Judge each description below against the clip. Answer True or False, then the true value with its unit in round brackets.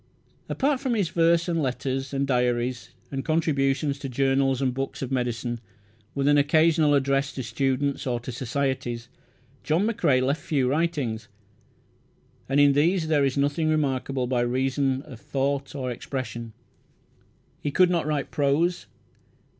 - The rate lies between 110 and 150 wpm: True (145 wpm)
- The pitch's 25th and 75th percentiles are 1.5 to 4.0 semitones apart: True (2.8 semitones)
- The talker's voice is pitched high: False (140 Hz)